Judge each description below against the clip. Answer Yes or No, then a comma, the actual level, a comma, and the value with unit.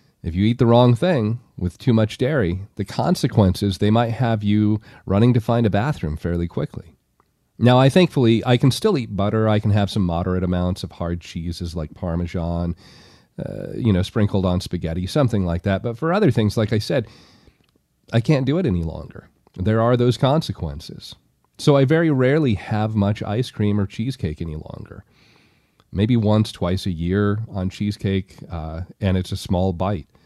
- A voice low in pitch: Yes, low, 105 Hz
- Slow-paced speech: No, average, 185 wpm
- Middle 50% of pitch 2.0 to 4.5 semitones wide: No, average, 4.9 semitones